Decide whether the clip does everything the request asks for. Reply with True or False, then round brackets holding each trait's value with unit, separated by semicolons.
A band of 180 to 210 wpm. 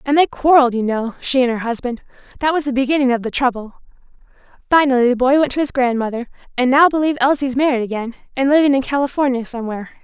True (195 wpm)